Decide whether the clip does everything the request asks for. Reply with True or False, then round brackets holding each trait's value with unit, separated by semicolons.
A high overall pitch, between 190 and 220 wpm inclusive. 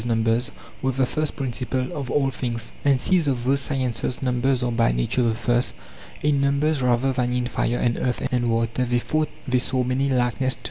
False (125 Hz; 205 wpm)